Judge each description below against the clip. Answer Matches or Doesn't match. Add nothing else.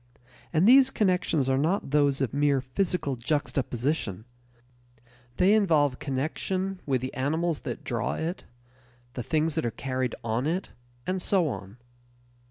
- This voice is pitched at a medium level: Matches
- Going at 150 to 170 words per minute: Doesn't match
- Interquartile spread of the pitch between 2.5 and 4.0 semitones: Doesn't match